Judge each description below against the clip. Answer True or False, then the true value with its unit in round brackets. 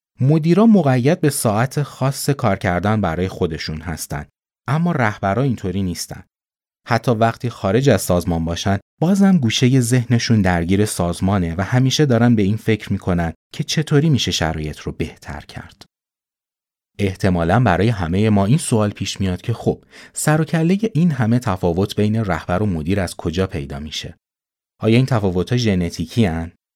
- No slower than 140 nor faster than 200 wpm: True (150 wpm)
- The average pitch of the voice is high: False (110 Hz)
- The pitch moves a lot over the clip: True (6.1 semitones)